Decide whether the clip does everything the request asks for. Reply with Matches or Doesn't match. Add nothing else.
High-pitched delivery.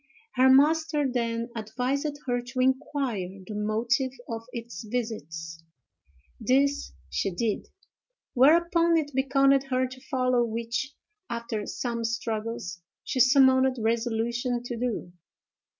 Matches